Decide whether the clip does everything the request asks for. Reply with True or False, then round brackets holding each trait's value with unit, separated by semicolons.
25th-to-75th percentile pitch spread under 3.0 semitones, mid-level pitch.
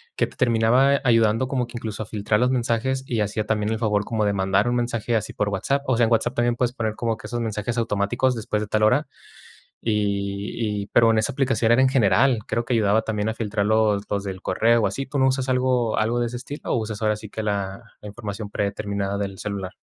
False (2.6 semitones; 110 Hz)